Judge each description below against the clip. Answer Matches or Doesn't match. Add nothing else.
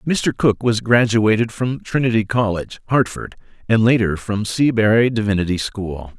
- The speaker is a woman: Doesn't match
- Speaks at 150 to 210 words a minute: Doesn't match